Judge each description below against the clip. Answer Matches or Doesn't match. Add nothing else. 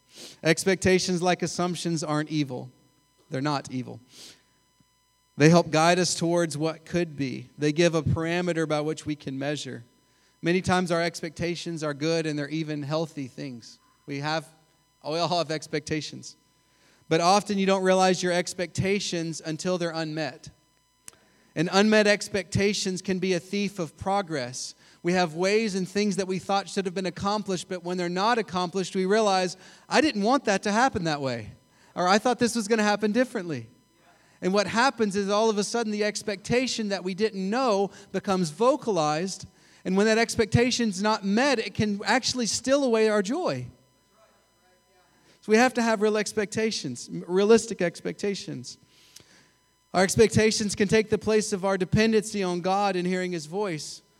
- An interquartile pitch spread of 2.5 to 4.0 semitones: Doesn't match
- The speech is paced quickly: Doesn't match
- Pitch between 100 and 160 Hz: Doesn't match